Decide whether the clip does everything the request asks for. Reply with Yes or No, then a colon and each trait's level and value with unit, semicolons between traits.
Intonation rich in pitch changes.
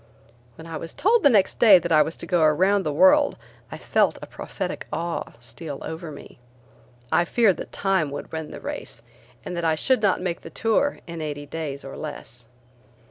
No: average, 4.1 semitones